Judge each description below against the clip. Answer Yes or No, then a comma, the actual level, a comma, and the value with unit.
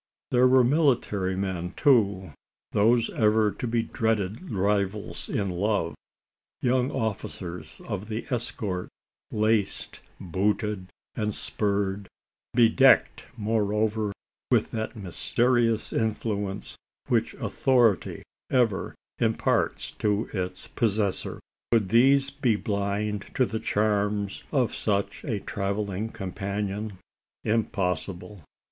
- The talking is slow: Yes, slow, 100 wpm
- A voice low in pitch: Yes, low, 105 Hz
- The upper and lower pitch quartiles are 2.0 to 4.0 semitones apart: Yes, narrow, 2.5 semitones